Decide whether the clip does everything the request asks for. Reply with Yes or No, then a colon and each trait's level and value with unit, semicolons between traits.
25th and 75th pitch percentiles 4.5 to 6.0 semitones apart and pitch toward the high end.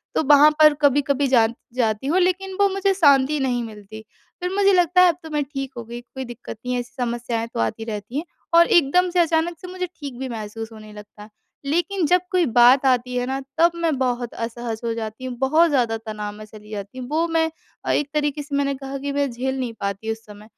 Yes: wide, 5.5 semitones; very high, 265 Hz